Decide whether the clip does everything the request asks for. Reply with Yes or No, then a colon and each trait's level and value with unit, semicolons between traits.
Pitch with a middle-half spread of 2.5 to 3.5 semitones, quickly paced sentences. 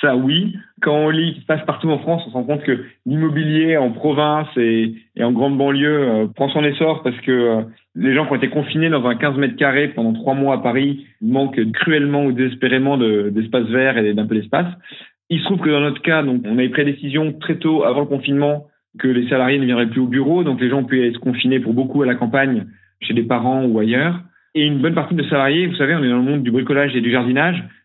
Yes: average, 3.2 semitones; fast, 260 wpm